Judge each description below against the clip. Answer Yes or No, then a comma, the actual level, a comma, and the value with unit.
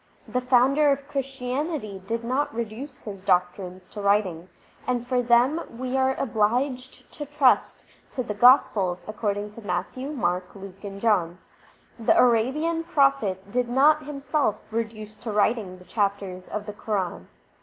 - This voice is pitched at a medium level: No, high, 230 Hz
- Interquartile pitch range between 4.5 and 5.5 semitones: Yes, average, 4.8 semitones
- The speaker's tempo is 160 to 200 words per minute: No, average, 145 wpm